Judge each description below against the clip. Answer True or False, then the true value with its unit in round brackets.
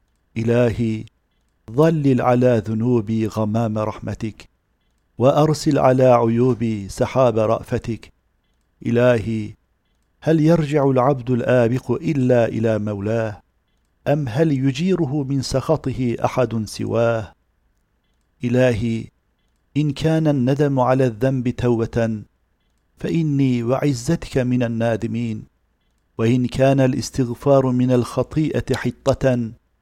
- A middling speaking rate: False (85 wpm)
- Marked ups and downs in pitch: False (3.2 semitones)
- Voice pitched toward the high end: False (120 Hz)